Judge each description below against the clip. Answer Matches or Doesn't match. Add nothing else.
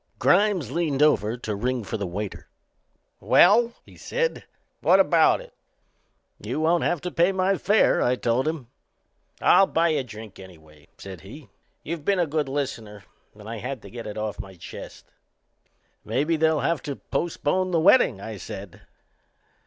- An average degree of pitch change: Doesn't match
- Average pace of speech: Matches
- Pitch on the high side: Doesn't match